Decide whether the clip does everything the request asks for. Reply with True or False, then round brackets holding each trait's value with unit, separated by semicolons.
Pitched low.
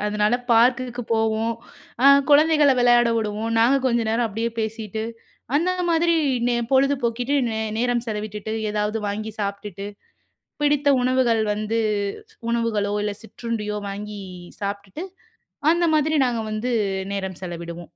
False (225 Hz)